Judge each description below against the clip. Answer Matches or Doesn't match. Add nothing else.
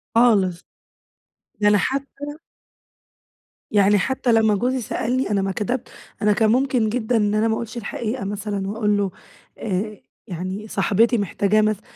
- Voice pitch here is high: Matches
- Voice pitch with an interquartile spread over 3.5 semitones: Doesn't match